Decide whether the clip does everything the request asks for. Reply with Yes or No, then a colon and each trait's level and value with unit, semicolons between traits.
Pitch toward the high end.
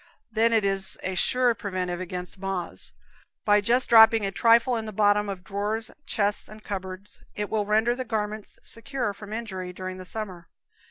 Yes: high, 210 Hz